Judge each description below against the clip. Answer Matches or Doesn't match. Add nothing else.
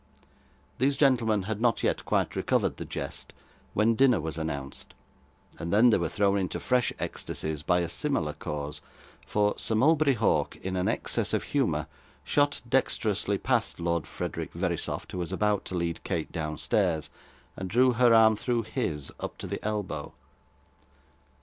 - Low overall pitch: Matches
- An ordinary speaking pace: Matches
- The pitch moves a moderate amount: Doesn't match